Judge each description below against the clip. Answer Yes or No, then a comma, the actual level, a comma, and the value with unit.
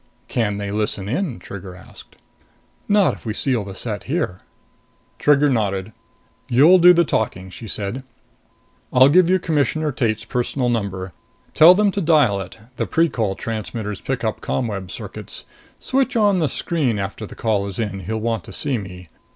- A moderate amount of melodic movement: No, wide, 7.0 semitones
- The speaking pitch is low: Yes, low, 115 Hz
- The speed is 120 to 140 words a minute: No, average, 165 wpm